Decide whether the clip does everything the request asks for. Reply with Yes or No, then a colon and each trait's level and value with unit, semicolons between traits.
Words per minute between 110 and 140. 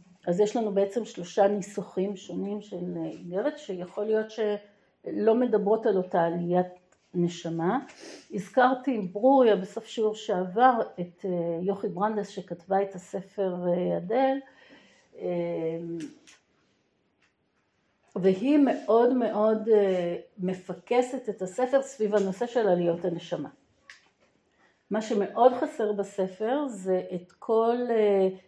No: slow, 100 wpm